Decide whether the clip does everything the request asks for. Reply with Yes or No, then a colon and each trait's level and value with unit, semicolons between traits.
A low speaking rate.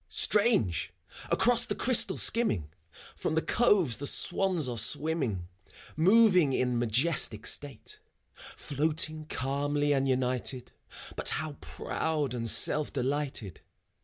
Yes: slow, 110 wpm